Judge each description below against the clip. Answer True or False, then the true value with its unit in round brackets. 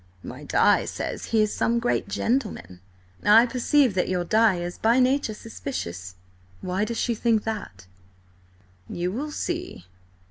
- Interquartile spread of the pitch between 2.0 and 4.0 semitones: False (5.2 semitones)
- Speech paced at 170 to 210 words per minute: False (145 wpm)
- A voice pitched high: True (220 Hz)